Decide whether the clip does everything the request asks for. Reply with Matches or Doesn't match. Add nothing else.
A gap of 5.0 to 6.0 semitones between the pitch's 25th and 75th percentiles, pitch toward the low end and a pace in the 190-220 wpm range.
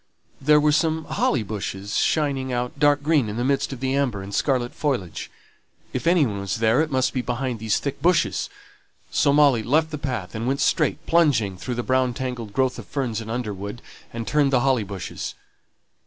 Doesn't match